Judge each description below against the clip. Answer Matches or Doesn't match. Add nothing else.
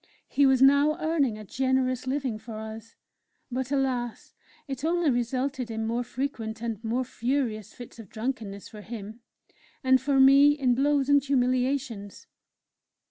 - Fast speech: Doesn't match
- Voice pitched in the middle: Doesn't match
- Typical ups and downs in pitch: Matches